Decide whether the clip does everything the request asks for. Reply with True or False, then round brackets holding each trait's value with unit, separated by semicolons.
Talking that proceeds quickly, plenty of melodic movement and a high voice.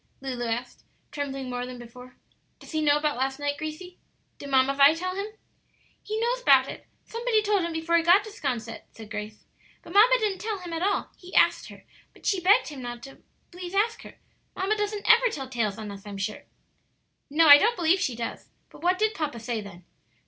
True (215 wpm; 7.9 semitones; 310 Hz)